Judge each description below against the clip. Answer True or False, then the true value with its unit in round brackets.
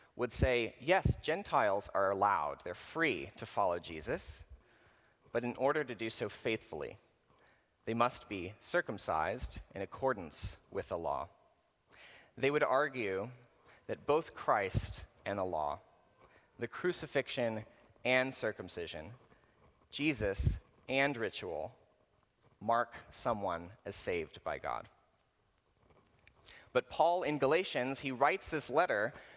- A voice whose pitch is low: True (120 Hz)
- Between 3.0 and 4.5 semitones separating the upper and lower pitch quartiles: True (3.4 semitones)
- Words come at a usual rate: False (115 wpm)